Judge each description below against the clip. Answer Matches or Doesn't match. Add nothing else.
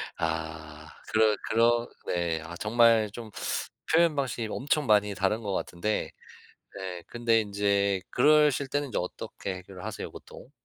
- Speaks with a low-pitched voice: Matches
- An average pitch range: Matches